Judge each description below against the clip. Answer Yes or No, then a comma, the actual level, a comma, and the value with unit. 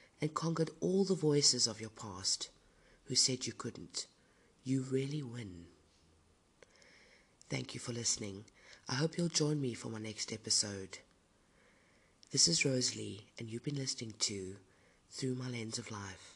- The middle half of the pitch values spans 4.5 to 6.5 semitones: Yes, average, 5.1 semitones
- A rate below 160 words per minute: Yes, average, 150 wpm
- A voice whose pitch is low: Yes, low, 115 Hz